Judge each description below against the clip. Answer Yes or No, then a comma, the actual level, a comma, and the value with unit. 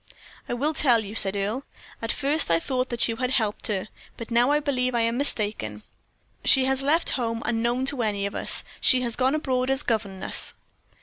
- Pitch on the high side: Yes, high, 240 Hz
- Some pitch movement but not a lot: Yes, average, 3.4 semitones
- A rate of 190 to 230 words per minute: Yes, average, 200 wpm